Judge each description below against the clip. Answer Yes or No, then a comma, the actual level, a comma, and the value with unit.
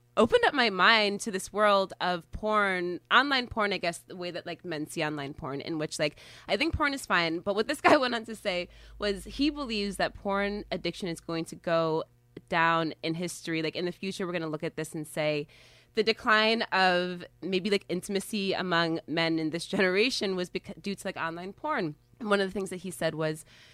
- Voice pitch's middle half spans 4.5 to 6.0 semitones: No, average, 4.0 semitones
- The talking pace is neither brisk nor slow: No, fast, 220 wpm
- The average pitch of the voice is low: No, medium, 180 Hz